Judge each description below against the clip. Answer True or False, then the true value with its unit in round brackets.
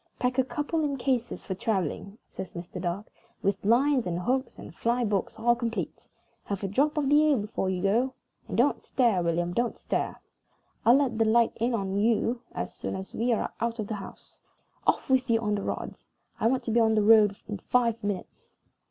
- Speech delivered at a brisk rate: True (210 wpm)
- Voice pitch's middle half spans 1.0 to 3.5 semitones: False (3.9 semitones)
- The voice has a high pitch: True (225 Hz)